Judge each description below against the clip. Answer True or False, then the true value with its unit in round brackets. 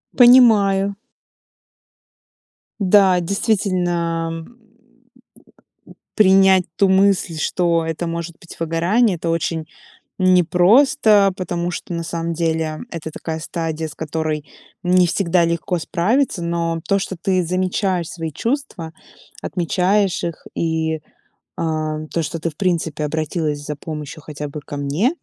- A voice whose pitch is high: False (170 Hz)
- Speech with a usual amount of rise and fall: True (3.0 semitones)